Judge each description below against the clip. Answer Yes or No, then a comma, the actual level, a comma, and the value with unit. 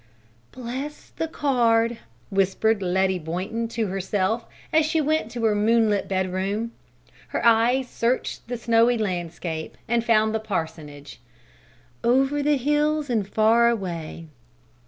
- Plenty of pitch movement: No, average, 4.2 semitones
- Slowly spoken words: Yes, slow, 125 wpm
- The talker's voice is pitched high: Yes, high, 225 Hz